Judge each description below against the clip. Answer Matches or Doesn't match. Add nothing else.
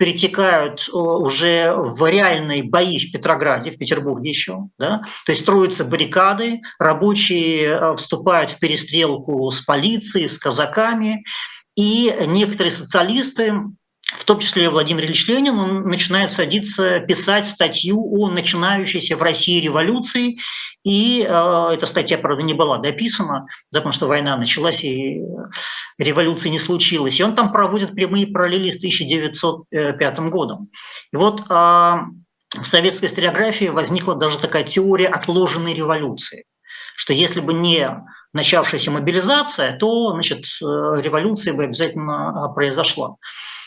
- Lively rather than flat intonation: Doesn't match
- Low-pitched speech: Doesn't match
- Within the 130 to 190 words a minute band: Doesn't match